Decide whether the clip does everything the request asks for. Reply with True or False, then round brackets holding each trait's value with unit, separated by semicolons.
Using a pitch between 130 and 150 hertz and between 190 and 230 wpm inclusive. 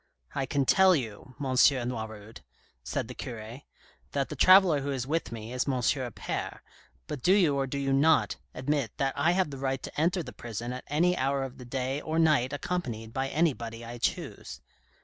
True (135 Hz; 205 wpm)